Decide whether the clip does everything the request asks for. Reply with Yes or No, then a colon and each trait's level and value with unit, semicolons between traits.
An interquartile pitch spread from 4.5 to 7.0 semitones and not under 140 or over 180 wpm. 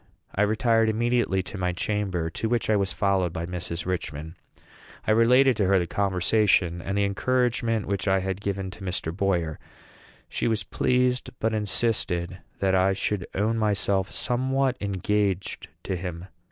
No: average, 3.2 semitones; average, 160 wpm